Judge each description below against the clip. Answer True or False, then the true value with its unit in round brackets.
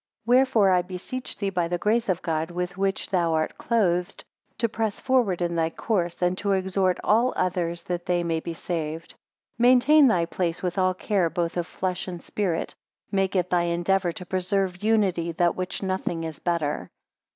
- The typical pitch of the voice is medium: True (180 Hz)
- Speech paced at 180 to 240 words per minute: True (190 wpm)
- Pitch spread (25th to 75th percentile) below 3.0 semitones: True (2.5 semitones)